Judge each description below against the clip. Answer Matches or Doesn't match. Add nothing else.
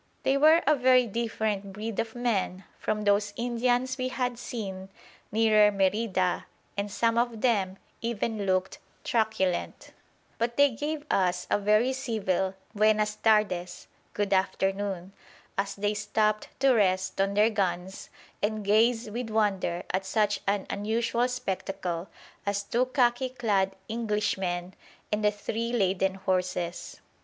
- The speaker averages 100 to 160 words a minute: Matches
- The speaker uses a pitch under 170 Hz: Doesn't match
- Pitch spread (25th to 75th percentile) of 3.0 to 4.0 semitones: Matches